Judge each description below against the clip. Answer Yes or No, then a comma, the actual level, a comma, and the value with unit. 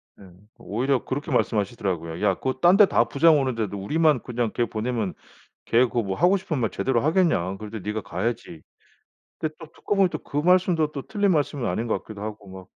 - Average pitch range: No, wide, 7.0 semitones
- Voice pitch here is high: No, low, 120 Hz